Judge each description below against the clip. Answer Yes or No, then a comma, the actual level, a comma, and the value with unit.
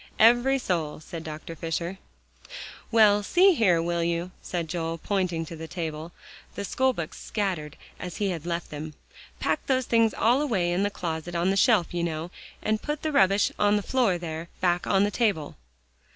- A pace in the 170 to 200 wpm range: Yes, average, 180 wpm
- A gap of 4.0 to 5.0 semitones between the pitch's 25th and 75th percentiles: Yes, average, 4.3 semitones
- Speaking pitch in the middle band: Yes, medium, 180 Hz